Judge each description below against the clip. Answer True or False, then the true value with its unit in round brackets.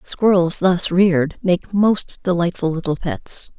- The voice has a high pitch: False (180 Hz)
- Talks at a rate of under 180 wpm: True (135 wpm)